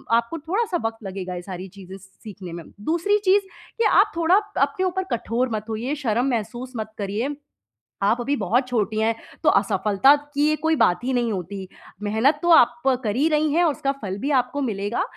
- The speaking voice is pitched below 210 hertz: No, high, 240 Hz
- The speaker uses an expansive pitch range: Yes, wide, 6.8 semitones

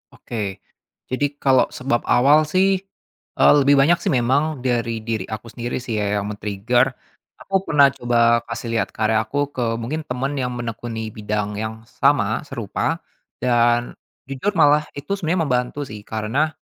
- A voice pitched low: Yes, low, 125 Hz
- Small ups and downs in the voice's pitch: No, average, 4.2 semitones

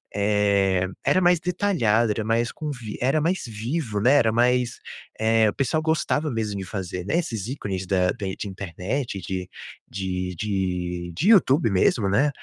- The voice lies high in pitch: No, low, 110 Hz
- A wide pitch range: Yes, wide, 6.1 semitones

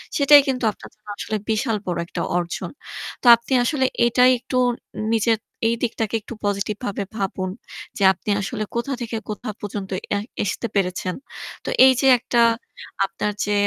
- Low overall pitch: No, high, 220 Hz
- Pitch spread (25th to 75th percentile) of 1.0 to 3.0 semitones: No, average, 3.4 semitones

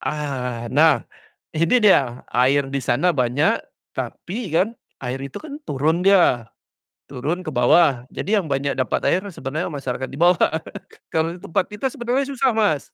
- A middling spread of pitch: No, wide, 5.8 semitones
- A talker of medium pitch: Yes, medium, 155 Hz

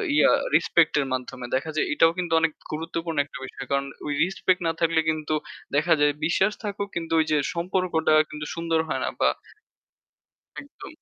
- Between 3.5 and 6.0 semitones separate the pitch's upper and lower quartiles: No, narrow, 2.5 semitones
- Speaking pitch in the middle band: Yes, medium, 160 Hz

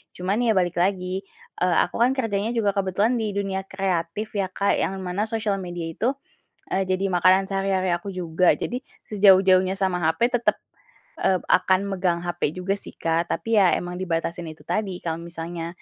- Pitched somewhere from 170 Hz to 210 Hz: Yes, high, 190 Hz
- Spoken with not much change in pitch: Yes, narrow, 2.3 semitones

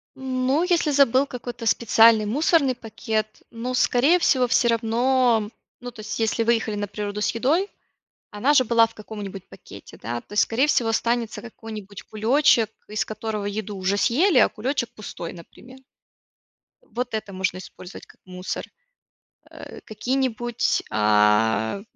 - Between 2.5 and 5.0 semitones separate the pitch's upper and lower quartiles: Yes, average, 3.5 semitones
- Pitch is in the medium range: No, high, 225 Hz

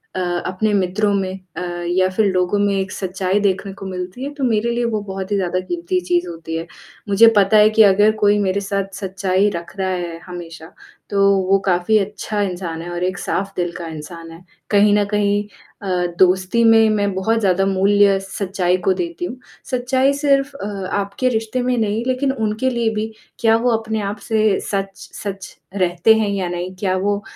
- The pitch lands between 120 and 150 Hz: No, high, 195 Hz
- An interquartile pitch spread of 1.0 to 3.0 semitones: Yes, average, 2.7 semitones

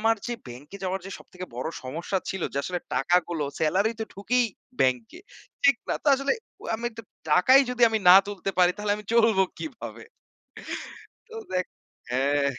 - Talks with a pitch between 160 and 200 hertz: Yes, high, 190 Hz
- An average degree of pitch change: No, wide, 6.0 semitones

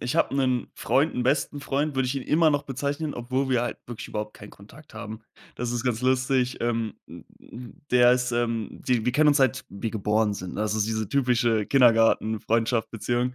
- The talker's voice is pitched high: No, low, 120 Hz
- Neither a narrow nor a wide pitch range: Yes, average, 3.0 semitones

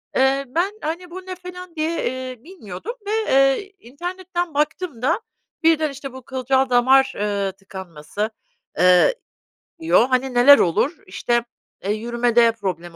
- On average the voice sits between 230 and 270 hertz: Yes, very high, 265 Hz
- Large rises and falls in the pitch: Yes, wide, 6.4 semitones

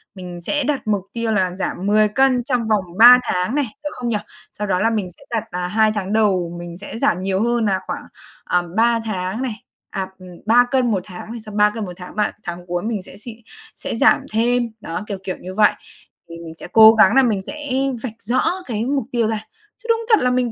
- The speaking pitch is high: Yes, high, 215 Hz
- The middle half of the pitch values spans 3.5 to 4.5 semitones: Yes, average, 4.1 semitones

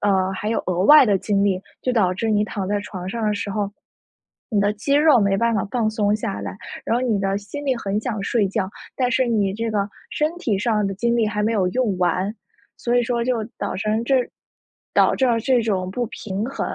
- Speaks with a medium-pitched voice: No, high, 215 Hz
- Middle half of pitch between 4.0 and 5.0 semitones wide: No, average, 3.2 semitones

